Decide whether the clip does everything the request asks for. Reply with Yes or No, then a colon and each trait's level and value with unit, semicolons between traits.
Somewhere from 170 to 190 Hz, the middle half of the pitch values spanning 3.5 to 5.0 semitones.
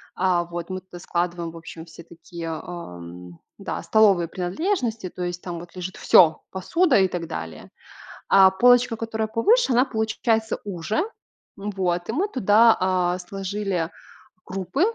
Yes: medium, 185 Hz; average, 4.3 semitones